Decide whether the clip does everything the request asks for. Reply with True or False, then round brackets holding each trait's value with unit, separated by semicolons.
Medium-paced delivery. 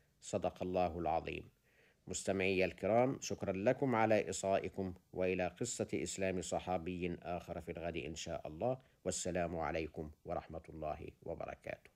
True (120 wpm)